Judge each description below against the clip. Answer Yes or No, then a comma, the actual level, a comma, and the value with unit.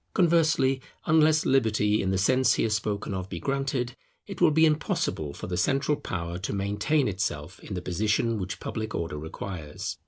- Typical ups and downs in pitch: No, wide, 6.6 semitones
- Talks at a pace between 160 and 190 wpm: Yes, average, 175 wpm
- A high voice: No, low, 105 Hz